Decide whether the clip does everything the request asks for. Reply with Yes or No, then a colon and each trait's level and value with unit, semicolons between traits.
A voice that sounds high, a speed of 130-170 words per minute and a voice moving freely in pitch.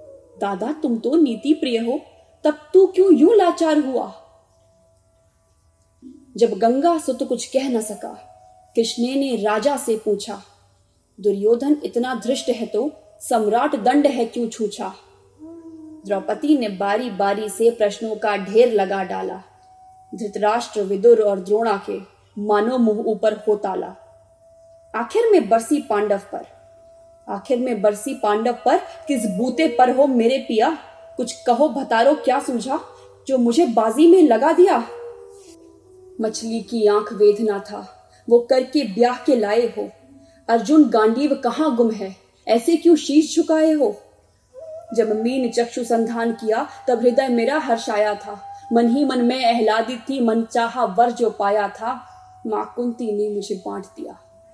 Yes: high, 240 Hz; average, 140 wpm; wide, 5.8 semitones